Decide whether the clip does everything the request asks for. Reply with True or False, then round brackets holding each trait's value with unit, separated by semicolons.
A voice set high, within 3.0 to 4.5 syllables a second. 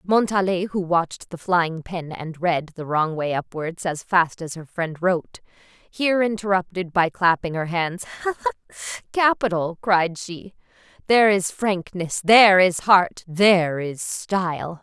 False (180 Hz; 4.2 syllables/s)